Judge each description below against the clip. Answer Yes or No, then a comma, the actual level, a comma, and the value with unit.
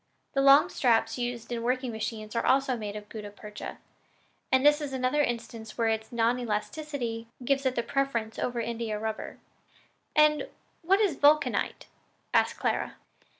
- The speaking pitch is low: No, high, 240 Hz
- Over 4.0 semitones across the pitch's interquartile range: No, average, 3.6 semitones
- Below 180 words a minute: Yes, average, 155 wpm